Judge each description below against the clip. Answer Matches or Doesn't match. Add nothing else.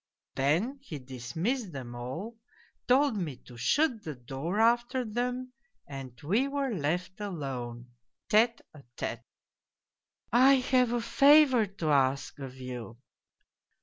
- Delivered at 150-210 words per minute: Doesn't match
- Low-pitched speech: Doesn't match